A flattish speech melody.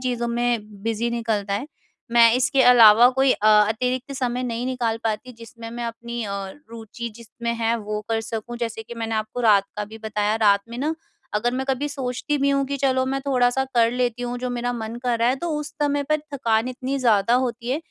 Yes: narrow, 2.3 semitones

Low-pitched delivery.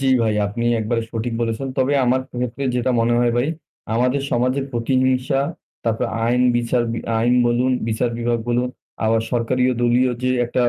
Yes: low, 120 Hz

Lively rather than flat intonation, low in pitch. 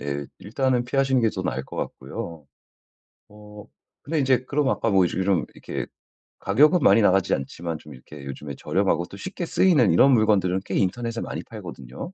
Yes: wide, 7.1 semitones; low, 100 Hz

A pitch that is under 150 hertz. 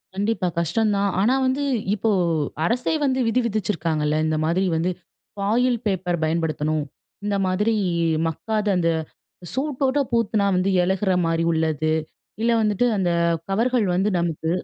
No: high, 195 Hz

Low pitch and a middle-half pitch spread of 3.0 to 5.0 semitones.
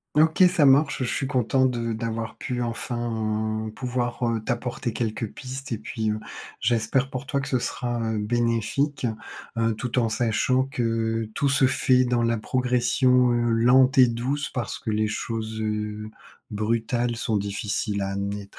No: low, 120 Hz; narrow, 2.5 semitones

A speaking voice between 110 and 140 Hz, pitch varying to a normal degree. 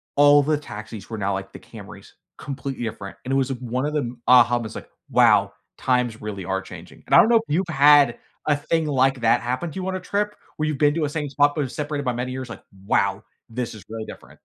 Yes: low, 135 Hz; average, 3.9 semitones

